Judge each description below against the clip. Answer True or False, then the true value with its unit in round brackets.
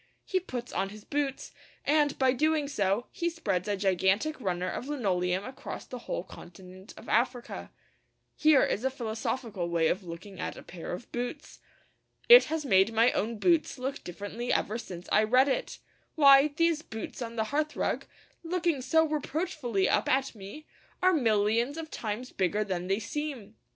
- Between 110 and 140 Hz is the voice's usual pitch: False (240 Hz)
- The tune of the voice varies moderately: False (6.8 semitones)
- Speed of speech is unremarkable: True (170 wpm)